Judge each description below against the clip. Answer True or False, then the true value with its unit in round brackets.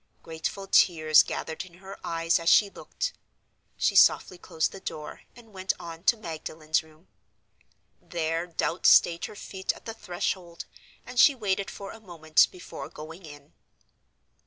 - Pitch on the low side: False (170 Hz)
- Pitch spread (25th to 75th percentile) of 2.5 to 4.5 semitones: True (3.3 semitones)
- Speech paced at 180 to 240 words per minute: False (155 wpm)